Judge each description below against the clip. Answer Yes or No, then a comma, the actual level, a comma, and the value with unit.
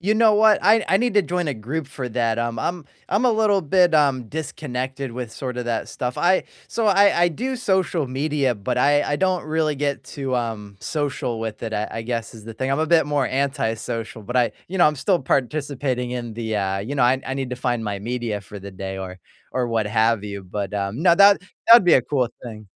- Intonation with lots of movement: Yes, wide, 5.9 semitones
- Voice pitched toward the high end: No, low, 130 Hz